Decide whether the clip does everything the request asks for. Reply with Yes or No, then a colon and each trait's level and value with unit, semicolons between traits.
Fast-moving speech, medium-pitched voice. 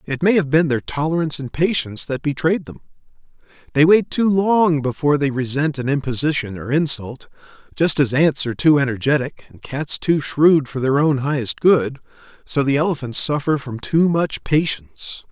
No: average, 175 wpm; medium, 145 Hz